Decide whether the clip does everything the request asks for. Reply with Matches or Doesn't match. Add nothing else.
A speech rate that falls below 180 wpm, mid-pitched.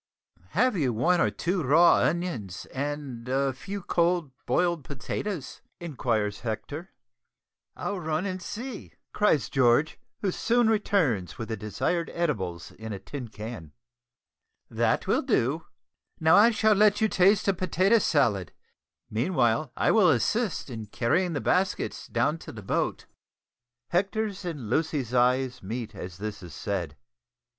Matches